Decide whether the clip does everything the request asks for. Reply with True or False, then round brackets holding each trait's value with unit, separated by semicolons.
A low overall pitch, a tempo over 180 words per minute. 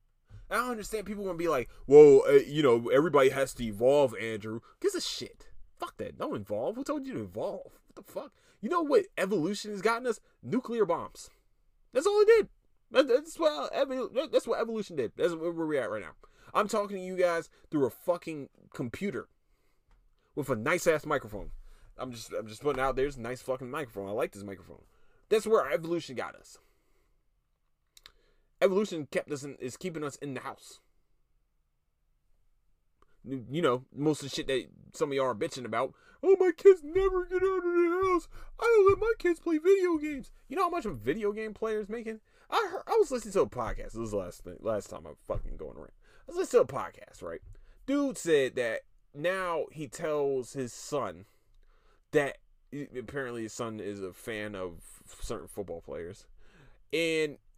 False (180 Hz; 195 wpm)